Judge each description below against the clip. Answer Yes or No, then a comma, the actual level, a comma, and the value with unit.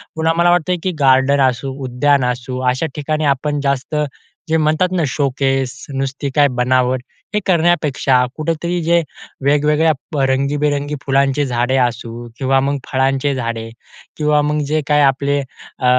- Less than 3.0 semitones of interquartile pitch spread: Yes, narrow, 2.5 semitones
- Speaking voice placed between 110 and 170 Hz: Yes, medium, 140 Hz